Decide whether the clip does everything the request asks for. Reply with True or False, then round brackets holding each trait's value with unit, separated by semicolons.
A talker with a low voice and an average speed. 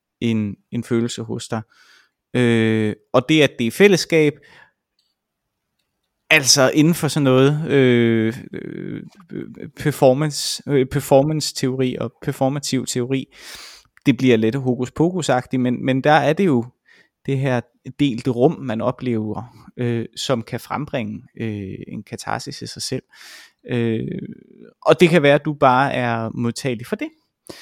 False (130 Hz; 135 wpm)